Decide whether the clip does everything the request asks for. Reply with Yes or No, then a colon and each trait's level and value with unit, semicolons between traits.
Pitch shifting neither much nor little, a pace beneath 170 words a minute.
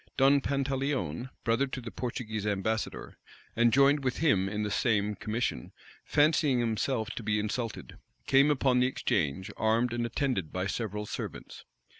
Yes: average, 4.2 semitones; average, 150 wpm